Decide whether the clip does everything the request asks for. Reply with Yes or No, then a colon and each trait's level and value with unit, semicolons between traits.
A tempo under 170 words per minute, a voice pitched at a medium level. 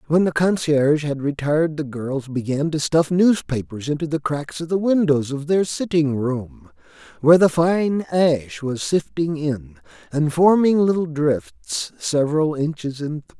Yes: average, 160 wpm; medium, 150 Hz